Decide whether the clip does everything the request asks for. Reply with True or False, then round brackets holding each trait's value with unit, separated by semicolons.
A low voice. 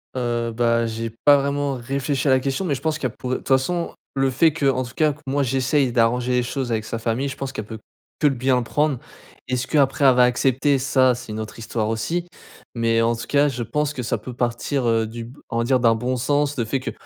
True (130 Hz)